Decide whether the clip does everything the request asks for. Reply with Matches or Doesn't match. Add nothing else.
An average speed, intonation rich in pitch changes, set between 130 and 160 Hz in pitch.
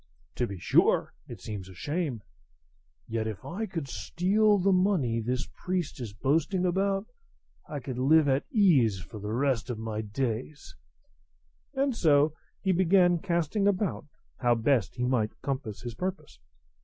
Matches